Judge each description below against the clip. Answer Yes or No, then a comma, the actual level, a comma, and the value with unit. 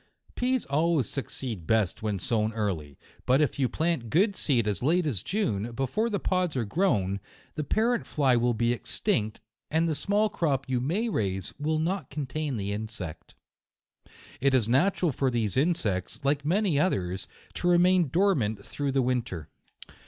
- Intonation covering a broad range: Yes, wide, 7.7 semitones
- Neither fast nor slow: Yes, average, 165 wpm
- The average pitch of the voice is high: No, low, 135 Hz